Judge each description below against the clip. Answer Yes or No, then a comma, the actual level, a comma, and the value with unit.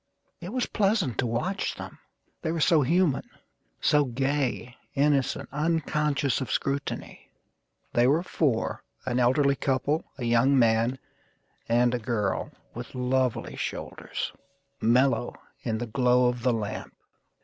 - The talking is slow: Yes, slow, 130 wpm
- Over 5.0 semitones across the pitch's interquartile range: No, average, 3.5 semitones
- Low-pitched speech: Yes, low, 130 Hz